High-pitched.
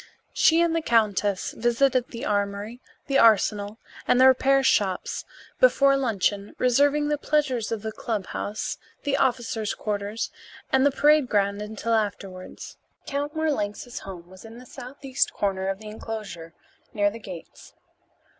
Yes: high, 225 Hz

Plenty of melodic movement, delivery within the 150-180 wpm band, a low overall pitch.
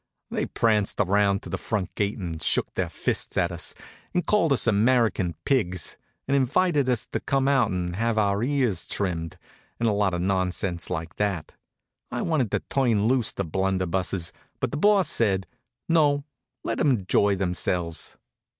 Yes: wide, 5.9 semitones; average, 170 wpm; low, 100 Hz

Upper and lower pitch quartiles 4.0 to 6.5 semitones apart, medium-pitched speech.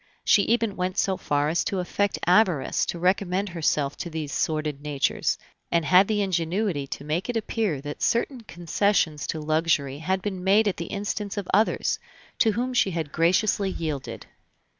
Yes: average, 4.6 semitones; medium, 180 Hz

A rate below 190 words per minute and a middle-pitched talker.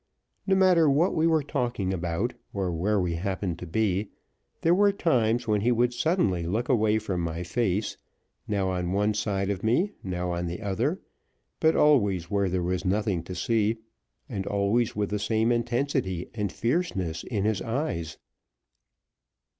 No: average, 165 wpm; low, 105 Hz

